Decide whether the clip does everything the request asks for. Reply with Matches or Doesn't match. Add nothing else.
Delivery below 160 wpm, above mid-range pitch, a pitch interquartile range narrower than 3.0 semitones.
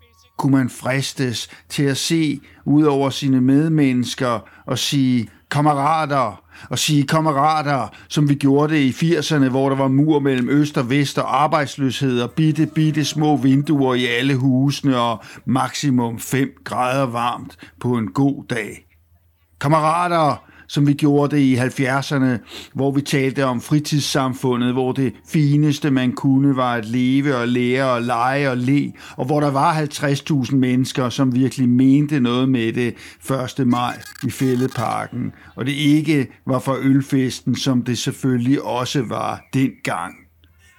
Doesn't match